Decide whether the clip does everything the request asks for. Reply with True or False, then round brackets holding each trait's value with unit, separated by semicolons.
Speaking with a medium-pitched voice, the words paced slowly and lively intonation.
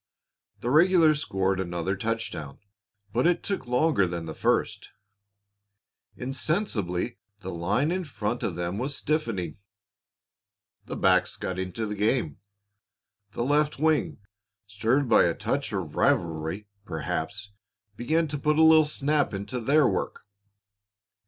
False (115 Hz; 130 wpm; 8.1 semitones)